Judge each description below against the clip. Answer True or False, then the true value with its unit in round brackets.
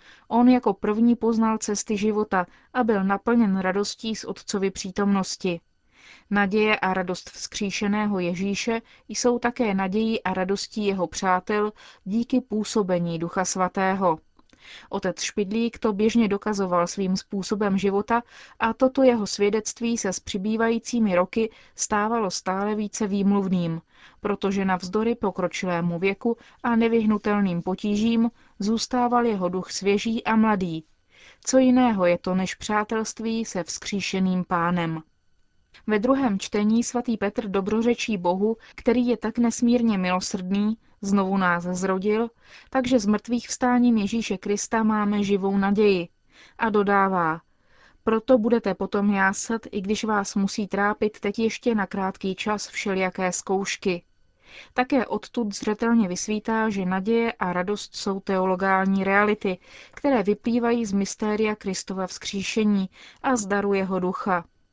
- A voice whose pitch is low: False (205 Hz)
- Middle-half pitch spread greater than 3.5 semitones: False (2.9 semitones)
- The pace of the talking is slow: False (125 wpm)